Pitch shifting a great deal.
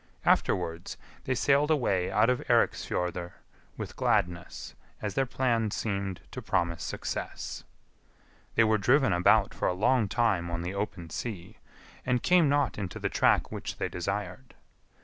Yes: wide, 6.0 semitones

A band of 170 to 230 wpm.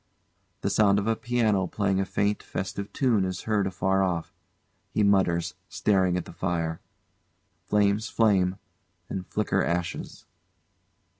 No: slow, 135 wpm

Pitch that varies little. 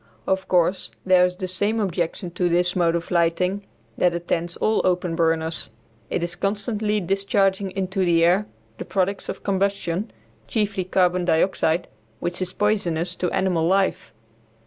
Yes: narrow, 2.2 semitones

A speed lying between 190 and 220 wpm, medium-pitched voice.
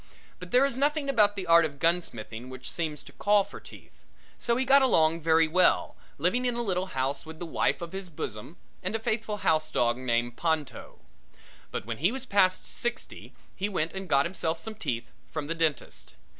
Yes: average, 200 wpm; medium, 170 Hz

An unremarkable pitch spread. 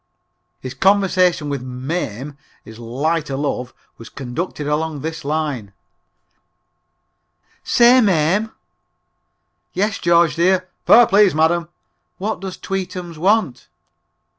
Yes: average, 5.0 semitones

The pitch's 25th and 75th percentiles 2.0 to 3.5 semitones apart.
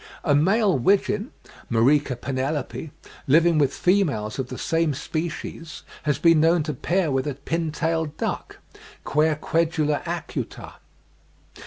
Yes: average, 3.1 semitones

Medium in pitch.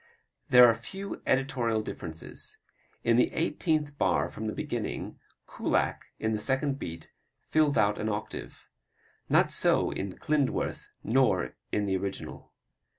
No: low, 115 Hz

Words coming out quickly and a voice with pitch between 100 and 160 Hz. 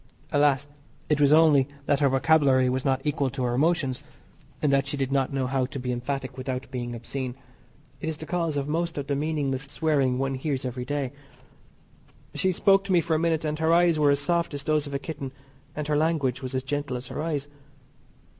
Yes: fast, 215 wpm; medium, 140 Hz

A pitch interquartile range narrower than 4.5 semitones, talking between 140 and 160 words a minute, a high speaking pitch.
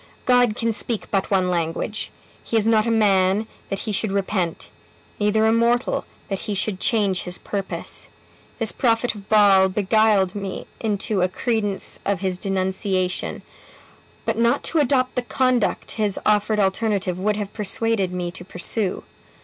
Yes: average, 2.8 semitones; average, 155 wpm; high, 205 Hz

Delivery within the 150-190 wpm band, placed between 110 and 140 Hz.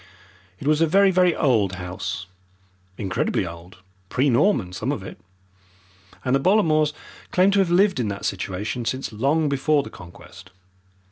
Yes: average, 155 wpm; low, 135 Hz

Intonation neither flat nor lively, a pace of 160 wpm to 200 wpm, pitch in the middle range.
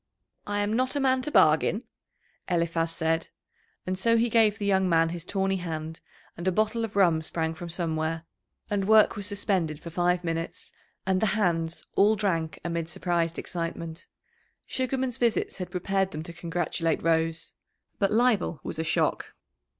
Yes: average, 3.8 semitones; average, 165 wpm; medium, 180 Hz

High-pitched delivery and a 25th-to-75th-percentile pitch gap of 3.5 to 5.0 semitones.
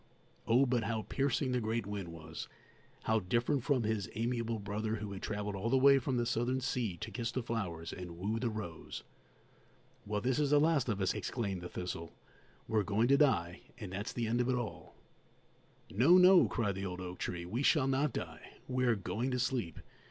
No: low, 115 Hz; average, 4.3 semitones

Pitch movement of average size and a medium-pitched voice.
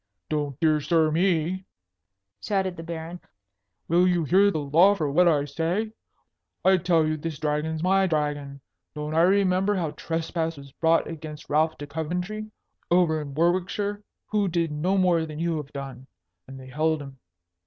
Yes: average, 3.2 semitones; medium, 165 Hz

